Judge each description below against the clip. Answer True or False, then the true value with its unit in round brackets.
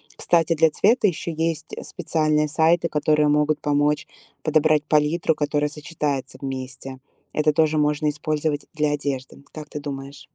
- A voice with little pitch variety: True (1.3 semitones)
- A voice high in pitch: False (150 Hz)